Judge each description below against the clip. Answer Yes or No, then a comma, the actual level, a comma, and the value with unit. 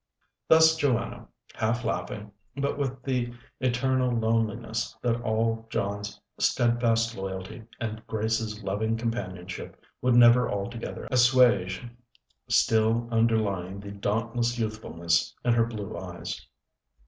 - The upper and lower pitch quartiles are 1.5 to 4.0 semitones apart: Yes, average, 2.8 semitones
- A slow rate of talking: Yes, slow, 110 wpm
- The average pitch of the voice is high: No, low, 115 Hz